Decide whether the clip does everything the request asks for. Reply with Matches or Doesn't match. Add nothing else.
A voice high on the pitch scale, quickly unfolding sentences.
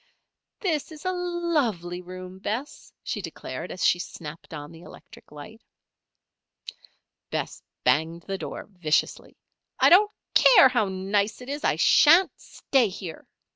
Doesn't match